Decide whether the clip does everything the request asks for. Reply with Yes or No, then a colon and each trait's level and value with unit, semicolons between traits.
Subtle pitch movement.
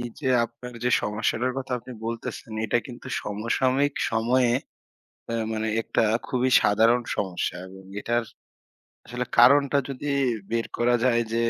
Yes: narrow, 2.1 semitones